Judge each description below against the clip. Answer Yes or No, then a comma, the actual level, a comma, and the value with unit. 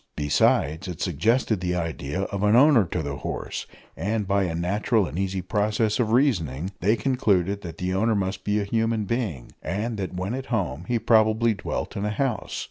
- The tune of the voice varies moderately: Yes, average, 3.9 semitones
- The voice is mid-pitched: No, low, 100 Hz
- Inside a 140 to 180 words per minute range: No, average, 195 wpm